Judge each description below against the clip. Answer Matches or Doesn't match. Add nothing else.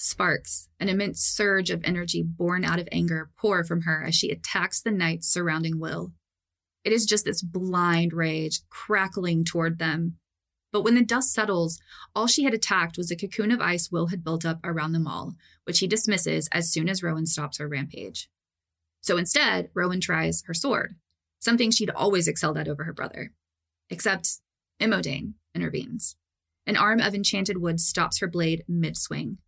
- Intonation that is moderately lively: Matches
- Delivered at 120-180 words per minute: Matches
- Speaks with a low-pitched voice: Doesn't match